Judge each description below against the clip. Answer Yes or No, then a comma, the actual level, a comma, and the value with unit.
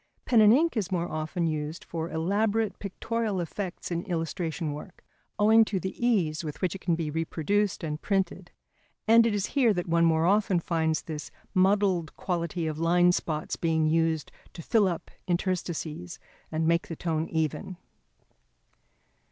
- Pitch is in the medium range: Yes, medium, 175 Hz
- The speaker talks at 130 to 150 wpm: No, average, 160 wpm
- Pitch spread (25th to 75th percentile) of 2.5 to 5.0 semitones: Yes, average, 3.6 semitones